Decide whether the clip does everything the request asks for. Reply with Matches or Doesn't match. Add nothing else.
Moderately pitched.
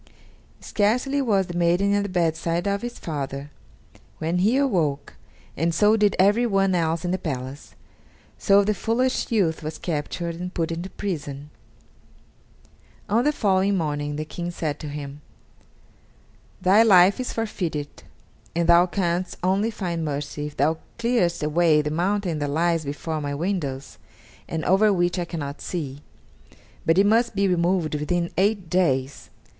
Matches